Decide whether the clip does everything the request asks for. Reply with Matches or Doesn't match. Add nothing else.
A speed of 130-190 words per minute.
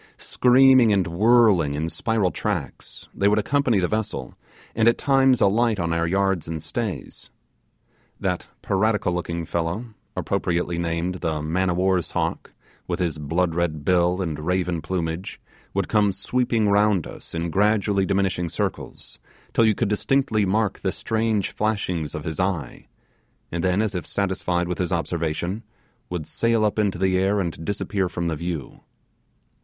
Matches